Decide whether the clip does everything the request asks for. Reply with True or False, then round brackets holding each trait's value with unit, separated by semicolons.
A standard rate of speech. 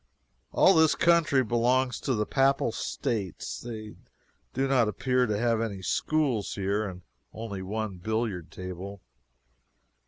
False (130 wpm)